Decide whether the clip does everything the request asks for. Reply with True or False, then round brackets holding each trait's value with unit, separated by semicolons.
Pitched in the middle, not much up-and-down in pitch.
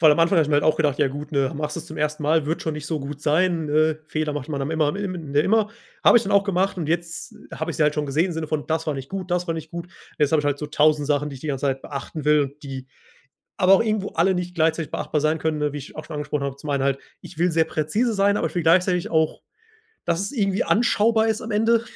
False (155 Hz; 3.3 semitones)